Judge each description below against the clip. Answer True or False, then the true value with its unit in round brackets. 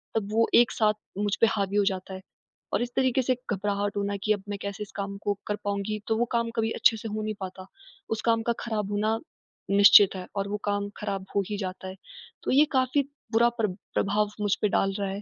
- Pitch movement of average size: False (1.9 semitones)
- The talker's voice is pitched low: False (205 Hz)